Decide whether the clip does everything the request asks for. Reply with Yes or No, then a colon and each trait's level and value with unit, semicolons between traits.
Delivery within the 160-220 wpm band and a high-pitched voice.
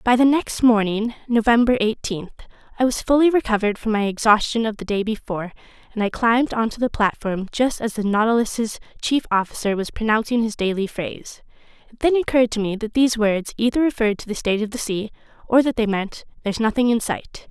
Yes: average, 200 wpm; high, 225 Hz